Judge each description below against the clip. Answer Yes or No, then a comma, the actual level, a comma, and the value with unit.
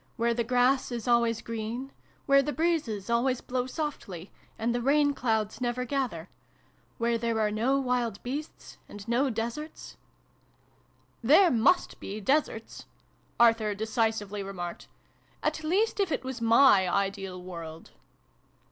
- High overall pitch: Yes, high, 235 Hz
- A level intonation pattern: No, average, 3.9 semitones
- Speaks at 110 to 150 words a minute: Yes, average, 140 wpm